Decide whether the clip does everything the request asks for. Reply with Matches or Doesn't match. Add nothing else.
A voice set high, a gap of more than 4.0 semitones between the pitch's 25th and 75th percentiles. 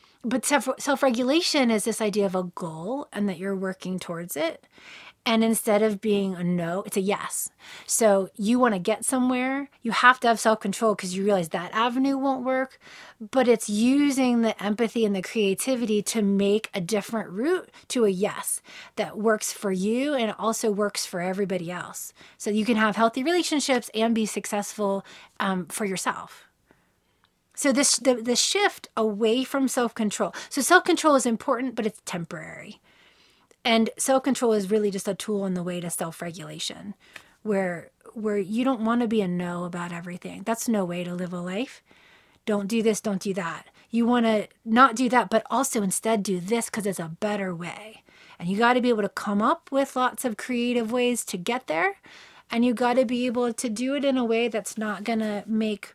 Doesn't match